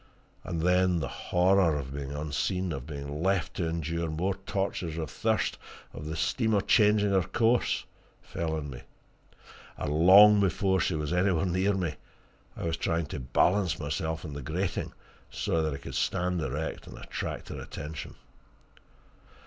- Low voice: Yes, very low, 85 Hz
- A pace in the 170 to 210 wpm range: No, average, 160 wpm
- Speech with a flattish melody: No, average, 3.7 semitones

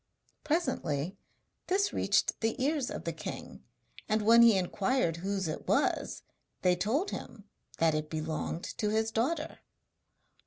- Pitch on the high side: Yes, high, 215 Hz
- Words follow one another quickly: No, average, 140 wpm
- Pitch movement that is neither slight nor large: No, wide, 7.2 semitones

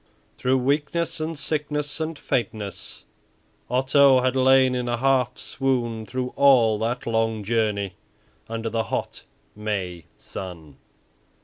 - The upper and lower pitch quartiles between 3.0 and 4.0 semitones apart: Yes, average, 3.4 semitones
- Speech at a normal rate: No, slow, 120 wpm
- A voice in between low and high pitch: No, low, 125 Hz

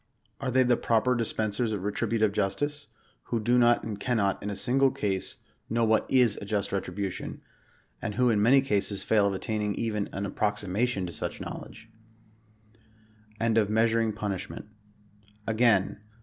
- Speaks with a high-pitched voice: No, low, 110 Hz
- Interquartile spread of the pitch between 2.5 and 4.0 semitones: Yes, average, 2.8 semitones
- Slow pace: No, average, 155 wpm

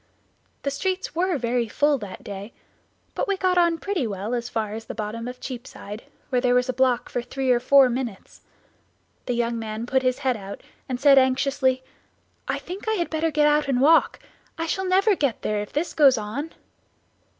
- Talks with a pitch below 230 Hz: No, very high, 260 Hz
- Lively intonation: No, average, 4.4 semitones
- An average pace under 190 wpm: No, average, 200 wpm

